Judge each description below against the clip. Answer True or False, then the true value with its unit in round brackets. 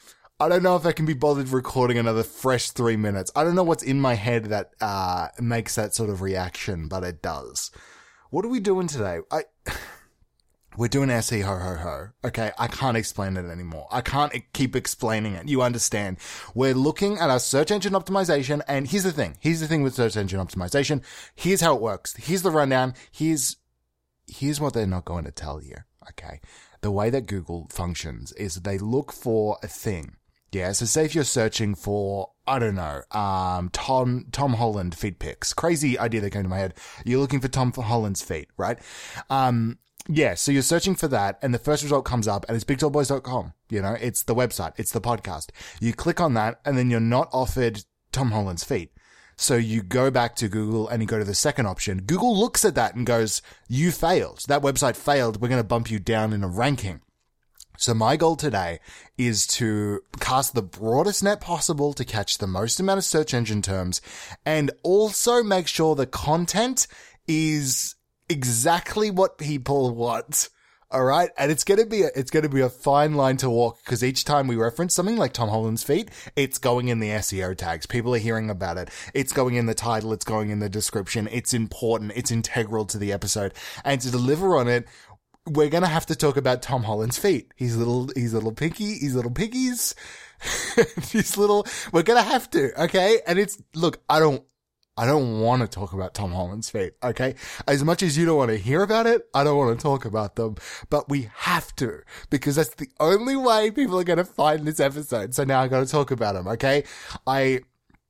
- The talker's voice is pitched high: False (125 Hz)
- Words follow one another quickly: True (210 wpm)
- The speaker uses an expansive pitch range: True (5.7 semitones)